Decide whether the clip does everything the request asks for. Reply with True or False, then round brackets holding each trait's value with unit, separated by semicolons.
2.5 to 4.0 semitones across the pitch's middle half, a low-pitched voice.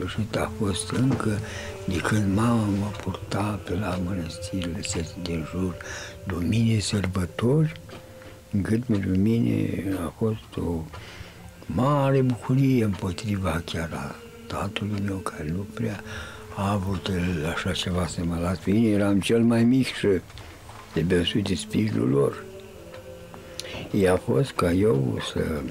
True (3.4 semitones; 100 Hz)